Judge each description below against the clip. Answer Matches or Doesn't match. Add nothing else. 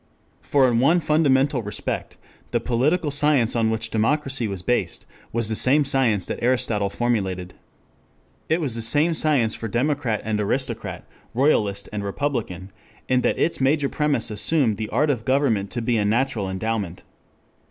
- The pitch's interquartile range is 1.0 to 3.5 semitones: Doesn't match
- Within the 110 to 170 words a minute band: Matches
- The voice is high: Doesn't match